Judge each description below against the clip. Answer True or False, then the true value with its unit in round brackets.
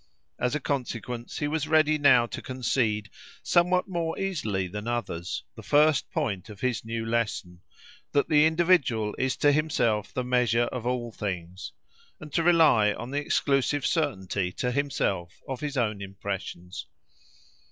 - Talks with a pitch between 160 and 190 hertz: False (125 Hz)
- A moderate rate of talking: True (150 wpm)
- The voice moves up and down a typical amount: False (5.8 semitones)